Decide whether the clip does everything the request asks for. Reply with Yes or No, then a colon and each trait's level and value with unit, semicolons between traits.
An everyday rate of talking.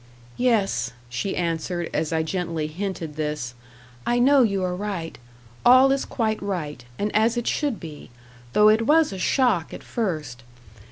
Yes: average, 160 wpm